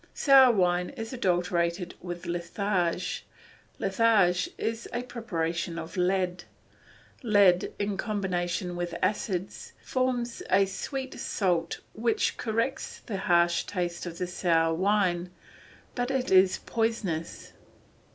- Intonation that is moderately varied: Yes, average, 4.3 semitones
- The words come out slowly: Yes, slow, 110 wpm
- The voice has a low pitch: No, medium, 185 Hz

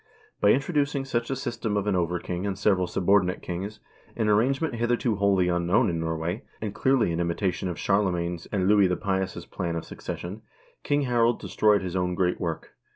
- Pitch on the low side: Yes, low, 100 Hz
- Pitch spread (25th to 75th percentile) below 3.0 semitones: No, average, 4.2 semitones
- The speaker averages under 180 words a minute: No, average, 190 wpm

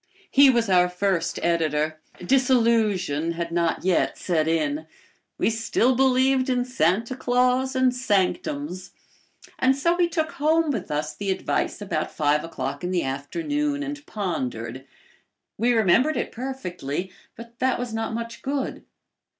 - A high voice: Yes, high, 225 Hz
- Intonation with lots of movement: Yes, wide, 7.5 semitones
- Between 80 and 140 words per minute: Yes, slow, 135 wpm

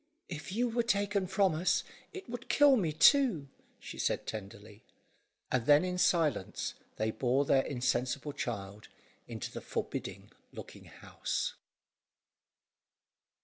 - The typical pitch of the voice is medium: Yes, medium, 155 Hz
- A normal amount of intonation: No, wide, 8.7 semitones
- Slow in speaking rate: Yes, slow, 125 wpm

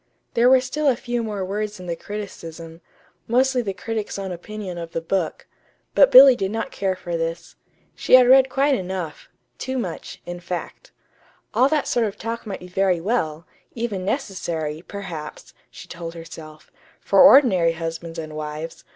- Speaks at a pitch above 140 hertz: Yes, high, 190 Hz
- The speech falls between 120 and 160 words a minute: No, average, 170 wpm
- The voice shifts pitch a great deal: Yes, wide, 5.8 semitones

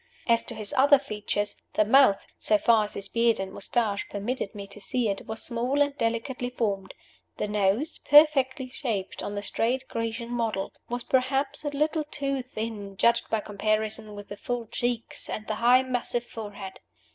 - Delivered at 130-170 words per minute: No, average, 180 wpm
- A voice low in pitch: No, high, 230 Hz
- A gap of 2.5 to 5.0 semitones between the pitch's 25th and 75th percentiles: Yes, average, 3.6 semitones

